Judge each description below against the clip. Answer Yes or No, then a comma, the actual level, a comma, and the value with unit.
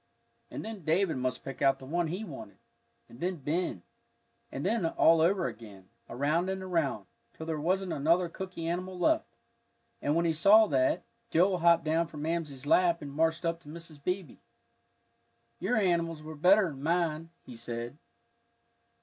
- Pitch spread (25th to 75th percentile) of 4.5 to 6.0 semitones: No, average, 3.8 semitones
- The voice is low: No, medium, 165 Hz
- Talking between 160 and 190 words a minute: Yes, average, 165 wpm